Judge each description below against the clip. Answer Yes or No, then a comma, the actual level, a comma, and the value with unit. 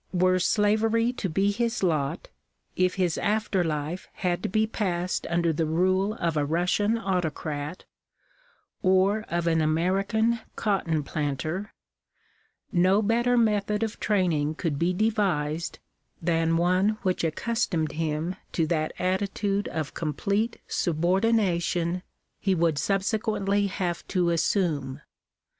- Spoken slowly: Yes, slow, 125 wpm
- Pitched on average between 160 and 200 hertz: Yes, medium, 185 Hz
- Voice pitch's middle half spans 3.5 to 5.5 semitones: Yes, average, 3.9 semitones